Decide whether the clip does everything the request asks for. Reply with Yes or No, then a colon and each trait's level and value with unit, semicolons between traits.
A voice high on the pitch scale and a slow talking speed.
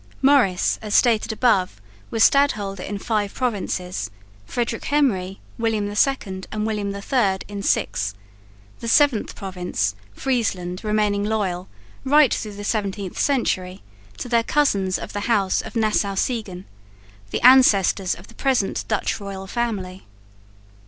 Yes: high, 205 Hz; slow, 130 wpm